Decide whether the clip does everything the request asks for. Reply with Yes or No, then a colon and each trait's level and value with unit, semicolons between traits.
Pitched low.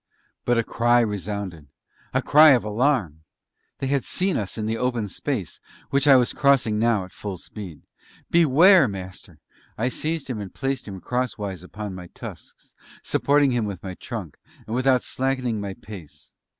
Yes: low, 115 Hz